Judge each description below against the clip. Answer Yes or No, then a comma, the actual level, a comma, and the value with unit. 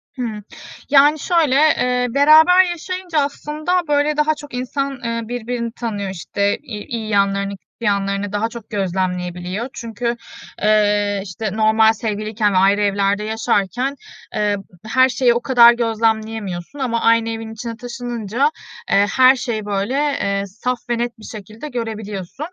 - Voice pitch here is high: Yes, high, 225 Hz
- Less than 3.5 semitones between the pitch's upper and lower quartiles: No, average, 3.9 semitones